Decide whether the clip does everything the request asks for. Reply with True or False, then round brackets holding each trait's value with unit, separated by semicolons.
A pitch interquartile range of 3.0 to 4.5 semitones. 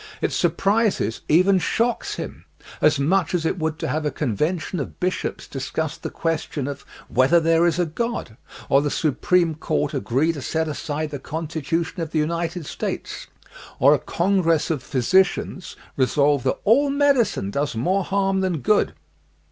True (4.0 semitones)